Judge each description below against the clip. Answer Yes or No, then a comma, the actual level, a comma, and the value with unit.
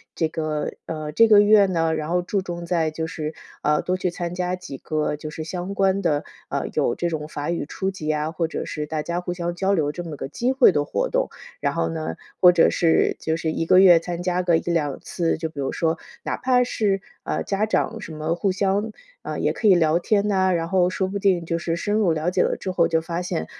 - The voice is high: No, medium, 170 Hz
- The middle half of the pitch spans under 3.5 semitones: Yes, average, 3.0 semitones